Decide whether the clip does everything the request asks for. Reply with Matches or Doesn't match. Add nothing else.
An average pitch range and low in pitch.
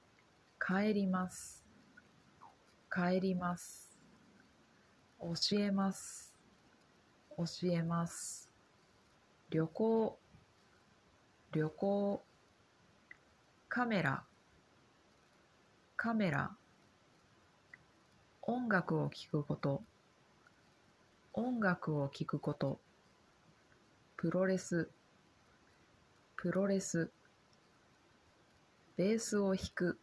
Doesn't match